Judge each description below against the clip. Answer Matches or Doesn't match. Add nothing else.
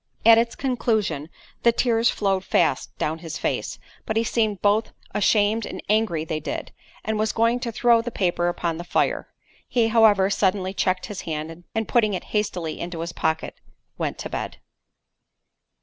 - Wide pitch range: Doesn't match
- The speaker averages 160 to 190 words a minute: Matches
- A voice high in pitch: Matches